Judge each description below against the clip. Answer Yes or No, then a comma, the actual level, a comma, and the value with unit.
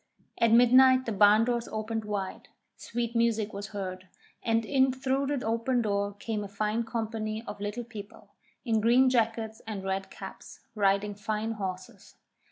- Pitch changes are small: Yes, narrow, 2.3 semitones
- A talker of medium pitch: No, high, 220 Hz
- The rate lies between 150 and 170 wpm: Yes, average, 160 wpm